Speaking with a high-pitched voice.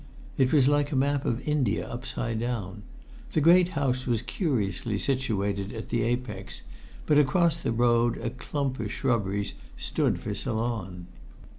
No: low, 120 Hz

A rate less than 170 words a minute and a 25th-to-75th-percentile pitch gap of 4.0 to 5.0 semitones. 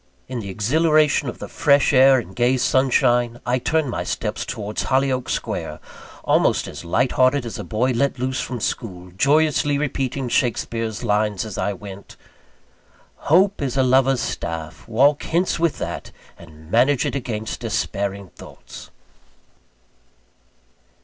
Yes: average, 145 wpm; average, 4.4 semitones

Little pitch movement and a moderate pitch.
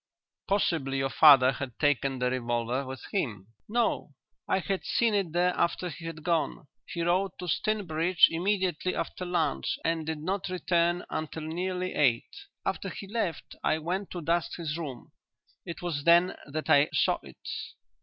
No: average, 4.1 semitones; medium, 165 Hz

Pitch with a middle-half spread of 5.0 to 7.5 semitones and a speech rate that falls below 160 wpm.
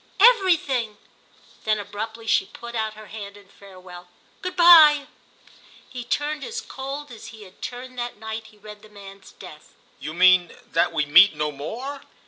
No: wide, 5.4 semitones; average, 165 wpm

